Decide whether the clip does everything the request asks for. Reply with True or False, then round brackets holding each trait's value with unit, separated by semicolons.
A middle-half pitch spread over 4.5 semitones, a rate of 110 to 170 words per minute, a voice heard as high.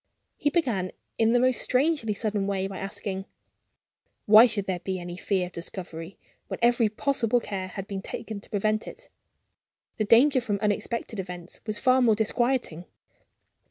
False (3.7 semitones; 160 wpm; 210 Hz)